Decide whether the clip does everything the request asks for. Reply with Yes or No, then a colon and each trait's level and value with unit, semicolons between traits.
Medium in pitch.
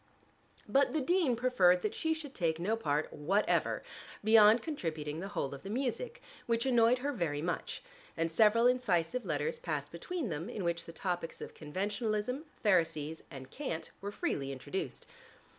No: high, 205 Hz